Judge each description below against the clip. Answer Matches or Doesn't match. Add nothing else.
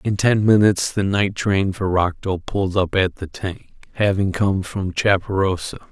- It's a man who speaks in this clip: Matches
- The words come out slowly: Doesn't match